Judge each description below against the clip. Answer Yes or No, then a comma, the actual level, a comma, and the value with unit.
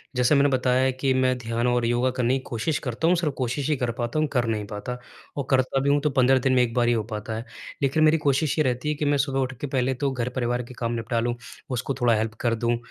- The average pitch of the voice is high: No, low, 125 Hz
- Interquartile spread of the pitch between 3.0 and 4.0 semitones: No, narrow, 2.4 semitones